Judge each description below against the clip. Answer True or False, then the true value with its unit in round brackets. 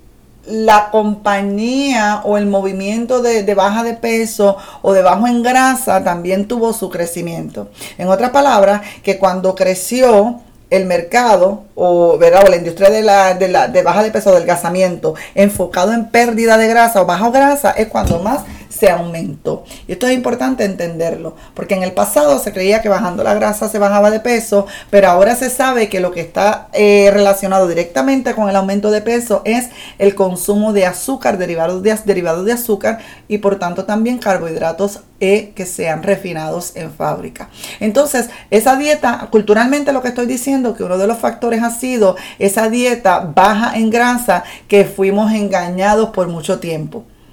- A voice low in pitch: False (205 Hz)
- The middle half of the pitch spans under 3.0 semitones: False (3.7 semitones)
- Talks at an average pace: True (170 wpm)